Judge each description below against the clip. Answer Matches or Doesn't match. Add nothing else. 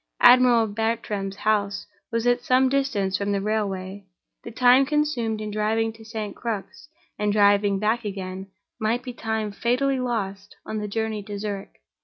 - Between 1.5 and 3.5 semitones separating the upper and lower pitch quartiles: Matches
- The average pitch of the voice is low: Doesn't match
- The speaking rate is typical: Matches